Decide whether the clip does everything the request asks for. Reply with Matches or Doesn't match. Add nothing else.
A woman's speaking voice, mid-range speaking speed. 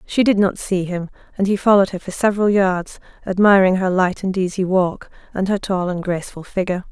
Doesn't match